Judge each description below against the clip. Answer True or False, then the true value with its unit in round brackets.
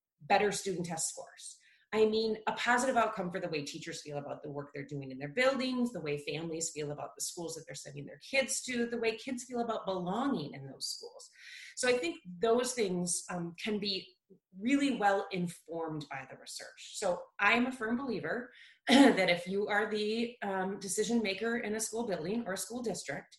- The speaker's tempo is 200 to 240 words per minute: True (205 wpm)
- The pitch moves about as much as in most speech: False (5.8 semitones)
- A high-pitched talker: True (200 Hz)